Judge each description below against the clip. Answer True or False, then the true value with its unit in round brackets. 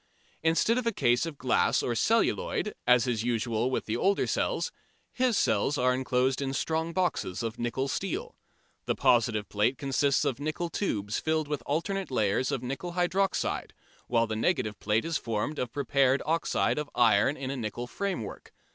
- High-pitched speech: False (135 Hz)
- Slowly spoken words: False (175 wpm)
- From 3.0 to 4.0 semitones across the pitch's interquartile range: False (5.6 semitones)